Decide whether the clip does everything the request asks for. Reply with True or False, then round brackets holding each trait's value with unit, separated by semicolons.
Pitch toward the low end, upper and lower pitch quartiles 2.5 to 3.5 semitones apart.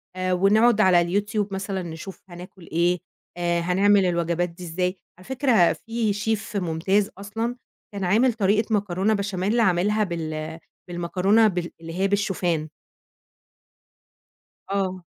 False (190 Hz; 3.1 semitones)